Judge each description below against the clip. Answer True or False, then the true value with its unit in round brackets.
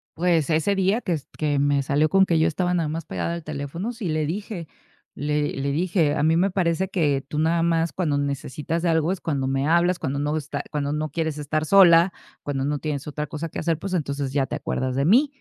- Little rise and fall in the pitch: False (3.0 semitones)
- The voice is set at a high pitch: False (155 Hz)